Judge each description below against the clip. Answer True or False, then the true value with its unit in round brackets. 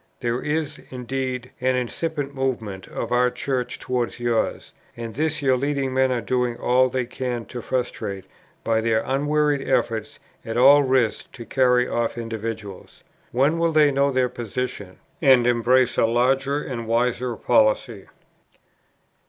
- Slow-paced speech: False (145 wpm)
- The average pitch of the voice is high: False (125 Hz)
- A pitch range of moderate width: False (2.3 semitones)